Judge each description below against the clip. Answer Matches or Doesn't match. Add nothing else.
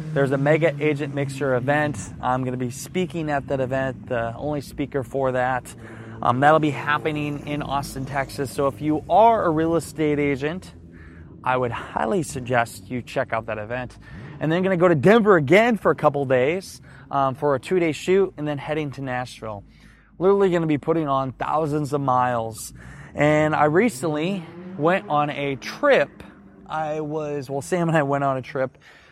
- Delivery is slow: Doesn't match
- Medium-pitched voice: Matches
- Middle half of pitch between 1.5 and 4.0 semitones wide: Matches